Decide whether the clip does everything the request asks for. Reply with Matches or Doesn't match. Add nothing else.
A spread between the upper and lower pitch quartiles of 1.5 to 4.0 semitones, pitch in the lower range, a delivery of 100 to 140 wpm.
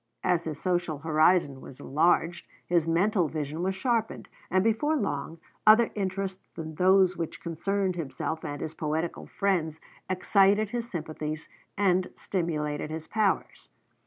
Doesn't match